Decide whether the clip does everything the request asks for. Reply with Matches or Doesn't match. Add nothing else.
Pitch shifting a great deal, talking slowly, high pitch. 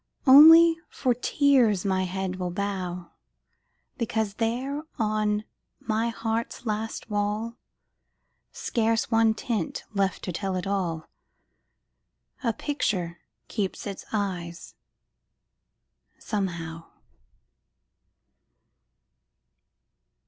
Doesn't match